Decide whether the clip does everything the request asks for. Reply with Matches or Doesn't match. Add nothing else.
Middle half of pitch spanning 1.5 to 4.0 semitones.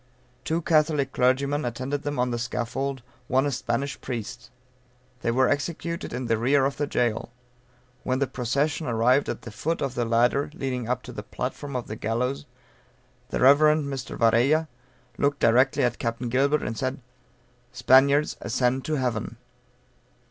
Matches